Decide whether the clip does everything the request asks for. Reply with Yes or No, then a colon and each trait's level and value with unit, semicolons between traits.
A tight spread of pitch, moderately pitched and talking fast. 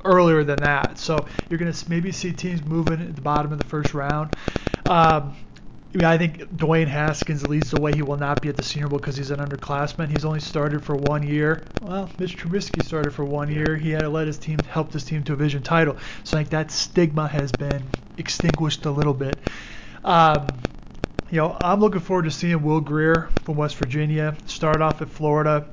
Yes: narrow, 1.9 semitones; medium, 155 Hz; fast, 220 wpm